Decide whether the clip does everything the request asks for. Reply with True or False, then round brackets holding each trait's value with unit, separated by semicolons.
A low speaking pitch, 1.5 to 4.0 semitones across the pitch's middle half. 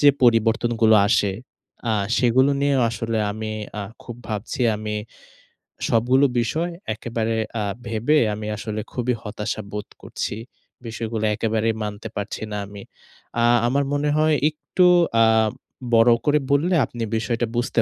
True (115 Hz; 2.8 semitones)